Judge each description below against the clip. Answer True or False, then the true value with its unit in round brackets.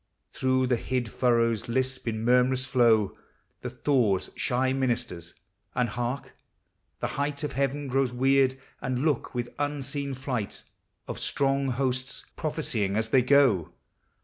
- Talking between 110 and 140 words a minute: True (135 wpm)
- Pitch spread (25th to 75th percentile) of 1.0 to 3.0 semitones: True (2.4 semitones)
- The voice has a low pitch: True (130 Hz)